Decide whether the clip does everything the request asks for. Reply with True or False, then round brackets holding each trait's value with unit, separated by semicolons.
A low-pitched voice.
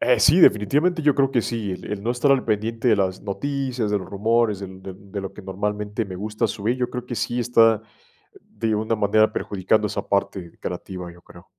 True (110 Hz)